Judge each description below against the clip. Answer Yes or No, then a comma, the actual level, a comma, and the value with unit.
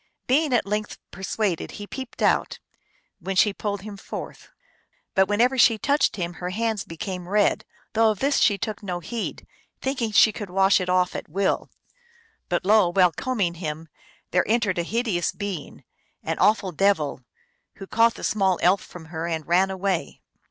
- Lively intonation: No, average, 3.4 semitones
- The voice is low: No, high, 195 Hz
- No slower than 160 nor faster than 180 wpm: Yes, average, 175 wpm